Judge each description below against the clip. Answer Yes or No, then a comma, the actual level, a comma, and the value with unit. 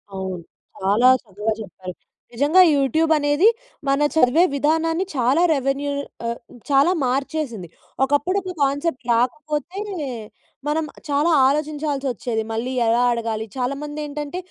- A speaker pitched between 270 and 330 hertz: Yes, very high, 280 Hz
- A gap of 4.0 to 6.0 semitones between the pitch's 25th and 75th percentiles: Yes, average, 4.4 semitones